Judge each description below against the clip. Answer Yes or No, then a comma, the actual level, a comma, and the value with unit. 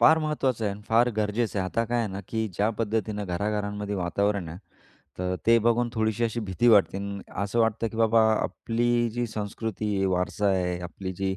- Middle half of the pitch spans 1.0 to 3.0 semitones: Yes, narrow, 2.6 semitones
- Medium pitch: No, low, 105 Hz